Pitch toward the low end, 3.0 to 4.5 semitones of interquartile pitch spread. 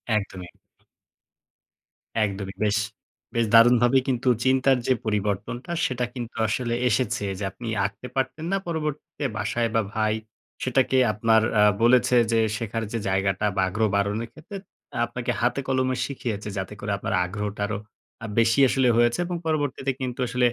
Yes: low, 115 Hz; average, 3.6 semitones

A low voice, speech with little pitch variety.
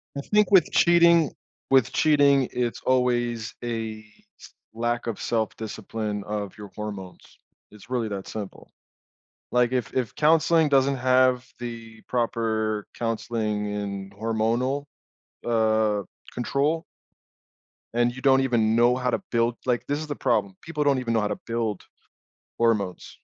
No: low, 120 Hz; average, 3.2 semitones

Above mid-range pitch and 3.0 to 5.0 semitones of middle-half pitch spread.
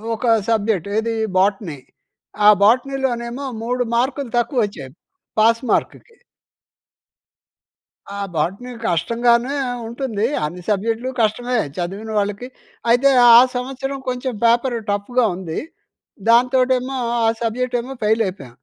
Yes: high, 235 Hz; average, 3.4 semitones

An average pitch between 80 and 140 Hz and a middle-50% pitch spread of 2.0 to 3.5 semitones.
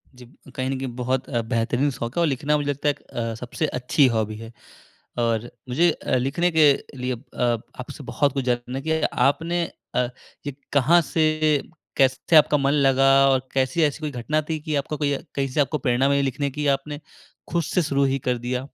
Yes: low, 135 Hz; average, 2.9 semitones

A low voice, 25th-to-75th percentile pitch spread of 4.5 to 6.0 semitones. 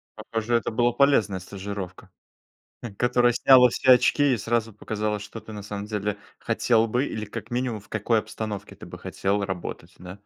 No: low, 110 Hz; average, 2.9 semitones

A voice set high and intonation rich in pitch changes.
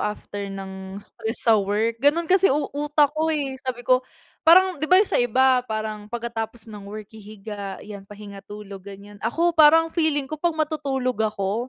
Yes: high, 230 Hz; wide, 6.3 semitones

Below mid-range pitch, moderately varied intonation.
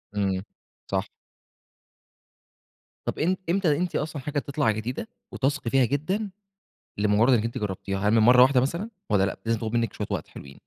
No: low, 125 Hz; wide, 5.7 semitones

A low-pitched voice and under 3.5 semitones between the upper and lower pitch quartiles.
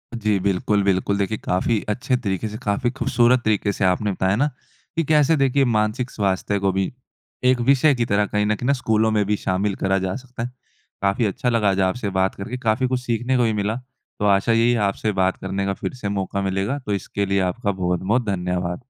No: low, 105 Hz; average, 3.8 semitones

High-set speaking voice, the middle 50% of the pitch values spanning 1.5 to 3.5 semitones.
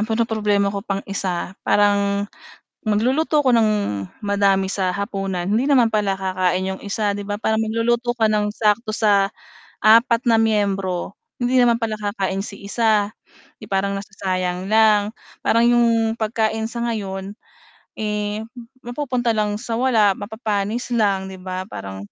Yes: high, 210 Hz; narrow, 2.5 semitones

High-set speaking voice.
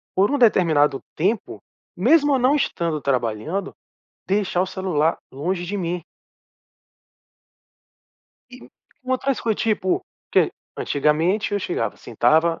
No: medium, 180 Hz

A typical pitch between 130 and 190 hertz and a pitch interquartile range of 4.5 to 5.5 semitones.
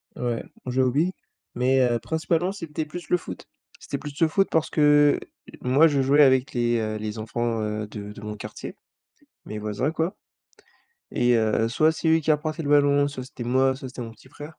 Yes: low, 135 Hz; average, 4.8 semitones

